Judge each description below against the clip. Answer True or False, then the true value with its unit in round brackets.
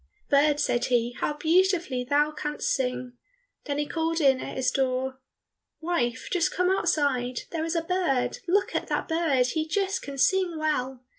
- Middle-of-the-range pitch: False (295 Hz)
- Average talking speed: True (170 wpm)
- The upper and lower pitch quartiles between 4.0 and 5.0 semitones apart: True (4.4 semitones)